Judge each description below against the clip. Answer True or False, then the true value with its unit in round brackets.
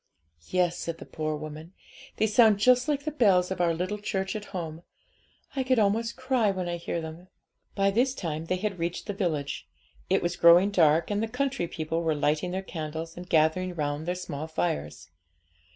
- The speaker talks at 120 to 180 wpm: False (195 wpm)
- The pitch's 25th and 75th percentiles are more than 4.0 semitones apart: True (4.5 semitones)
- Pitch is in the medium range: True (180 Hz)